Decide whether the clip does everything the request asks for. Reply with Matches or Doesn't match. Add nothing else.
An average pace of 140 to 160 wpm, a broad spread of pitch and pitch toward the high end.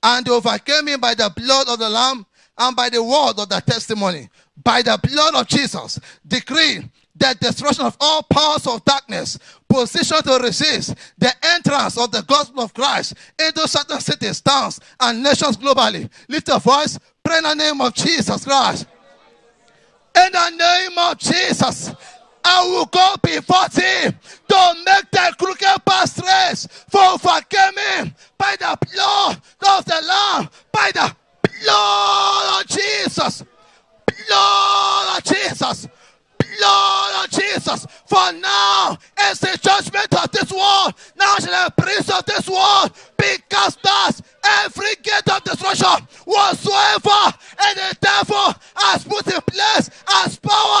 Matches